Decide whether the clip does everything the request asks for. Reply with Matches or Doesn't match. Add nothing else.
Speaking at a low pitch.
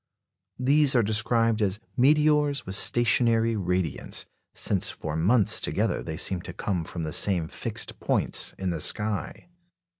Matches